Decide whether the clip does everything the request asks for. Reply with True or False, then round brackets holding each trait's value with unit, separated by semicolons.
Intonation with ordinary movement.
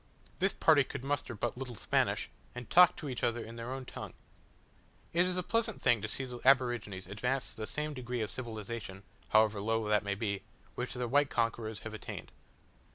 True (3.6 semitones)